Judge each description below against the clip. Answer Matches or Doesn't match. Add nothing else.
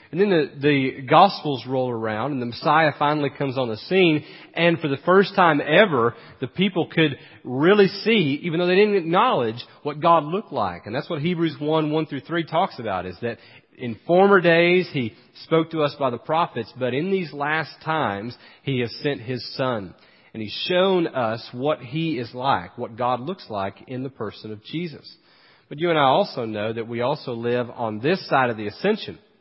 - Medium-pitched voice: Matches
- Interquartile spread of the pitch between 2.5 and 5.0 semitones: Doesn't match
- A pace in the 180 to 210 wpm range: Matches